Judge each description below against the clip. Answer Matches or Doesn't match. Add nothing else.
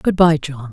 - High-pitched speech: Doesn't match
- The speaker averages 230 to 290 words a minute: Matches